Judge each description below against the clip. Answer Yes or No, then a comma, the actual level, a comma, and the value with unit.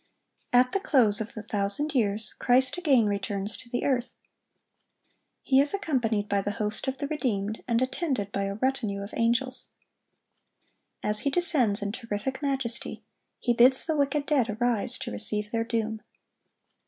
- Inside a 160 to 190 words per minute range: Yes, average, 165 wpm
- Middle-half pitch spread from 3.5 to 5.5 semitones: Yes, average, 4.2 semitones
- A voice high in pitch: Yes, high, 235 Hz